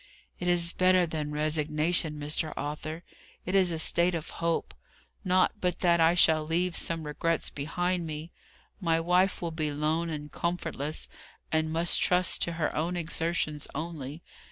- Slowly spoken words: No, average, 155 wpm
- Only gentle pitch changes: Yes, narrow, 2.2 semitones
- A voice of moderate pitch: Yes, medium, 165 Hz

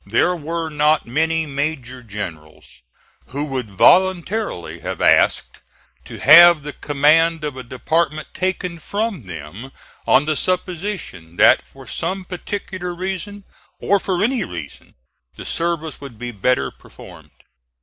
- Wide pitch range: Yes, wide, 6.0 semitones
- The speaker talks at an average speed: No, slow, 130 wpm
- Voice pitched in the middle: Yes, medium, 155 Hz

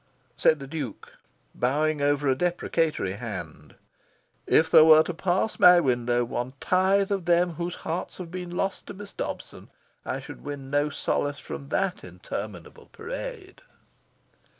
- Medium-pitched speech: Yes, medium, 155 Hz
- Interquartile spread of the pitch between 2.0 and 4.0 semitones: No, wide, 5.5 semitones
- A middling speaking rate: Yes, average, 150 wpm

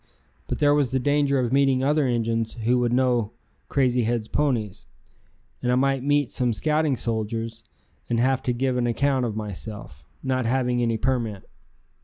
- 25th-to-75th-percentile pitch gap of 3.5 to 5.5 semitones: No, average, 2.7 semitones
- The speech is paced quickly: No, average, 170 wpm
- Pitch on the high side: No, low, 125 Hz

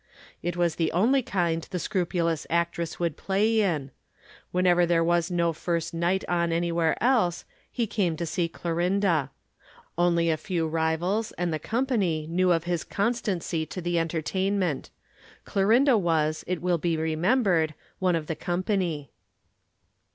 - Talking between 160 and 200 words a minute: No, average, 145 wpm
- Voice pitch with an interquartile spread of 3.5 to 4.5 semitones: No, narrow, 2.4 semitones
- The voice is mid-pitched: Yes, medium, 175 Hz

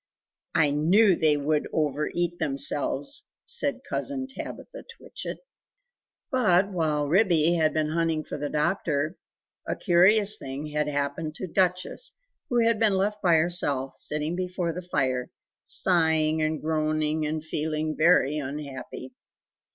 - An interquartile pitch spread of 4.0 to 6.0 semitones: No, average, 3.2 semitones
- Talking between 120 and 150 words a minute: Yes, slow, 135 wpm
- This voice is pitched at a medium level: Yes, medium, 160 Hz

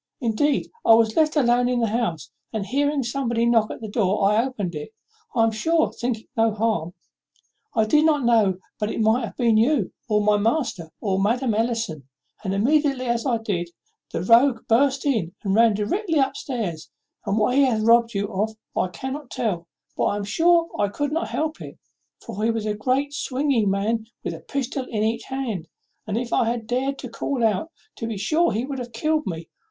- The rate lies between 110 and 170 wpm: No, fast, 205 wpm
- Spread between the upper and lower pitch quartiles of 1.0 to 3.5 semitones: No, average, 4.1 semitones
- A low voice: No, high, 230 Hz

